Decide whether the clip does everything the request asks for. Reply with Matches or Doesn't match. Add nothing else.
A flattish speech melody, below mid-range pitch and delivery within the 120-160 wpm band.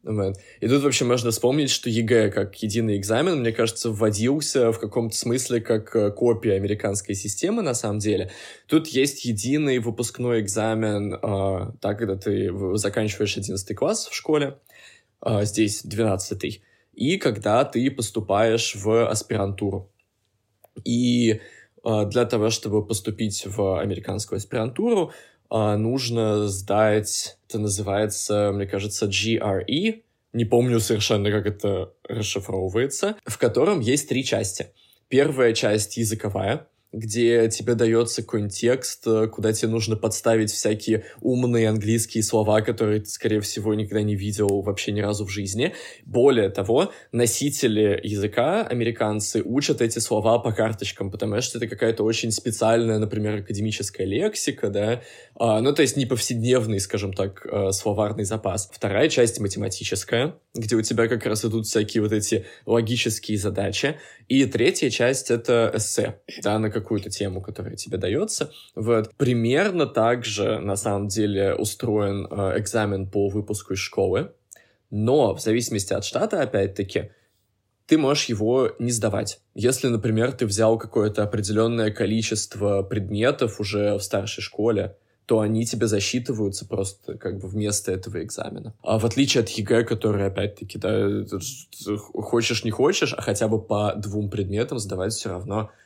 Matches